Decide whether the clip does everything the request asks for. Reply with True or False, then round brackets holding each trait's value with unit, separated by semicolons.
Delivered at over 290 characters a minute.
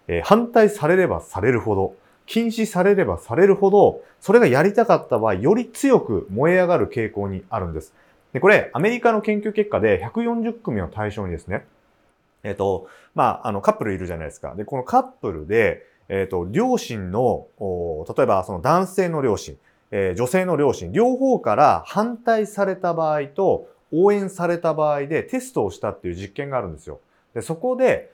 True (350 characters per minute)